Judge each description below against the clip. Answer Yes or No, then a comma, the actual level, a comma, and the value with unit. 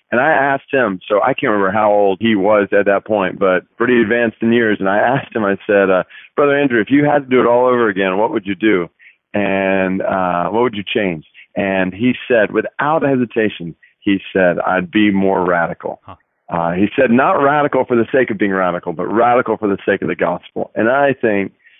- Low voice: Yes, low, 105 Hz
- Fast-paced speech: Yes, fast, 225 wpm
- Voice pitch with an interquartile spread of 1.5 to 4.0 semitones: No, average, 4.4 semitones